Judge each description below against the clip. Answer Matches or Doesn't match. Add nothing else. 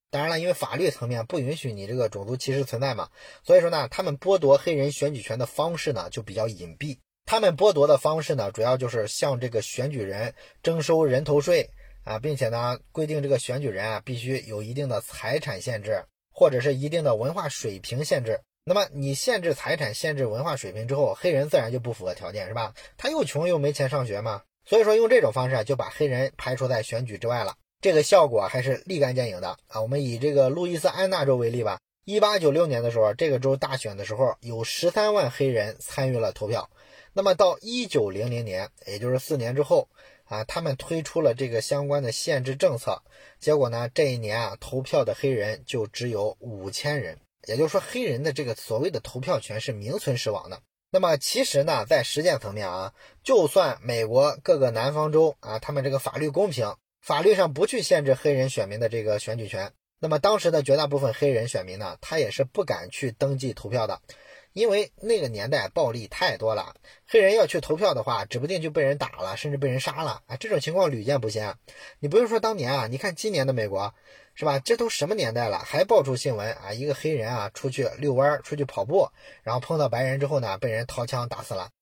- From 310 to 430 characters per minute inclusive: Matches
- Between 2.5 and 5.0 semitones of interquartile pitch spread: Matches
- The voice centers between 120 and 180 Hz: Matches